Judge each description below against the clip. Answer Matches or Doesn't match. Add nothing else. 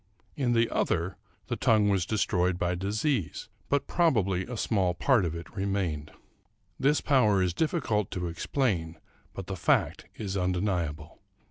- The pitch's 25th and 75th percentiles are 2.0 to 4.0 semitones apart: Doesn't match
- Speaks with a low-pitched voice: Matches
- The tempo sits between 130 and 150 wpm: Matches